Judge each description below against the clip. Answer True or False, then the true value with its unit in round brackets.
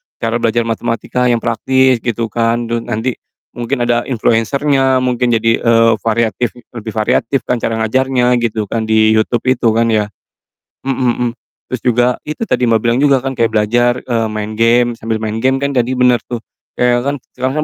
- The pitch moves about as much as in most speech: False (1.8 semitones)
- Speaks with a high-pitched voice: False (120 Hz)